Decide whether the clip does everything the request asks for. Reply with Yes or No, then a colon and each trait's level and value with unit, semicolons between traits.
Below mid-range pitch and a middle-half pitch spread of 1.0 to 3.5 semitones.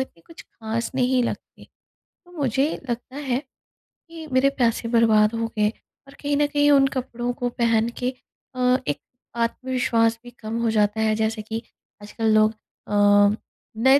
No: high, 235 Hz; average, 3.0 semitones